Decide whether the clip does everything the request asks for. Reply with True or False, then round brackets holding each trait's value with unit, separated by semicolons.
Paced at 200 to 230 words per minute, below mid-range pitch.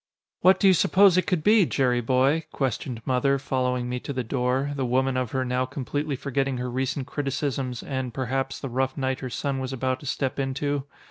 True (205 wpm; 130 Hz)